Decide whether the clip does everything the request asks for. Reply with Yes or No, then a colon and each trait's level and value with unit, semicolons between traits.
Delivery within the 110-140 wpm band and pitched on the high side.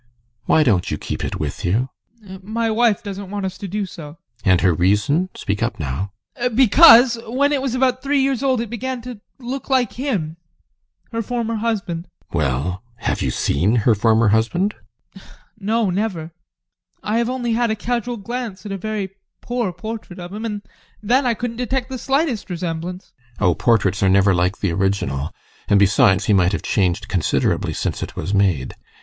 No: average, 190 wpm; high, 195 Hz